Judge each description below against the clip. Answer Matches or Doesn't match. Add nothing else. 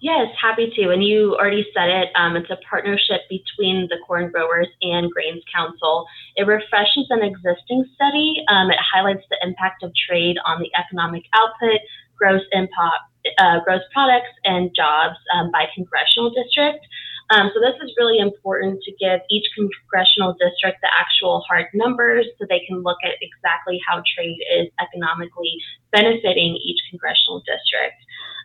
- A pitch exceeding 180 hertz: Matches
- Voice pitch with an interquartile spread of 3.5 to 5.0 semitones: Matches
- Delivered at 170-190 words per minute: Doesn't match